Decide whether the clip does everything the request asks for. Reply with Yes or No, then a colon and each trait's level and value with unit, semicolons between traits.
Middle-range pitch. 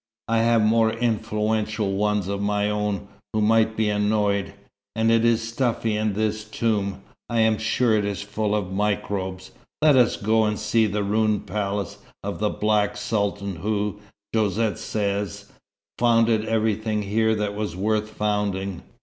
No: low, 105 Hz